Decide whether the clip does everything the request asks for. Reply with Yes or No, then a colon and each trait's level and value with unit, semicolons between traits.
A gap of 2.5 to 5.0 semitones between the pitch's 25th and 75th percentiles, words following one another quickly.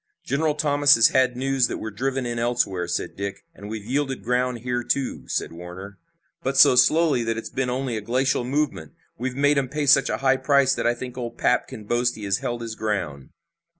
Yes: average, 3.4 semitones; fast, 215 wpm